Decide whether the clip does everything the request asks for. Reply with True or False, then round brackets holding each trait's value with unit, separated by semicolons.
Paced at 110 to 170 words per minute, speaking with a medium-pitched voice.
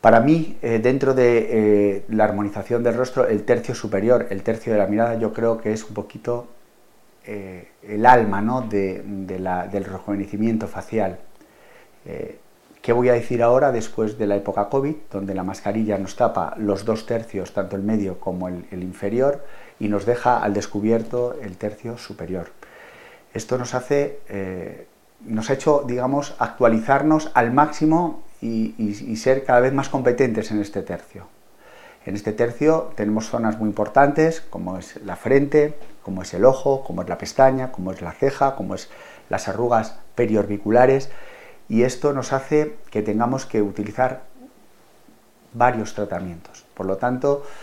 False (165 wpm; 115 Hz)